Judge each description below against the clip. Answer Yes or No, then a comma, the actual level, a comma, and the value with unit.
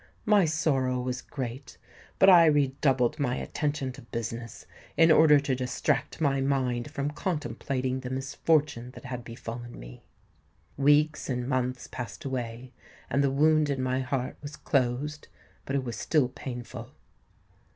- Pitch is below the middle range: Yes, low, 130 Hz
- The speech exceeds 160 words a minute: No, average, 145 wpm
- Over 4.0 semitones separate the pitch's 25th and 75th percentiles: No, average, 2.9 semitones